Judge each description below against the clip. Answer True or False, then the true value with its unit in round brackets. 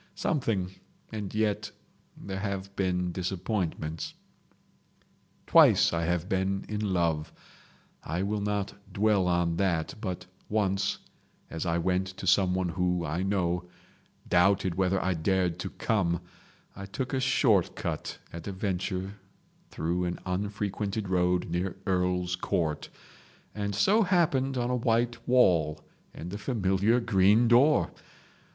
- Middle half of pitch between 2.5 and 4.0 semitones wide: True (2.9 semitones)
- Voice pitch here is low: True (95 Hz)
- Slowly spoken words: True (125 wpm)